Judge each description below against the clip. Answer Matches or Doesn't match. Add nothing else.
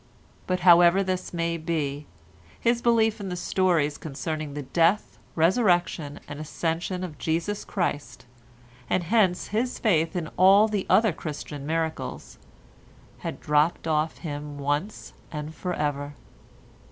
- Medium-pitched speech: Matches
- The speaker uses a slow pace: Matches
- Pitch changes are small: Doesn't match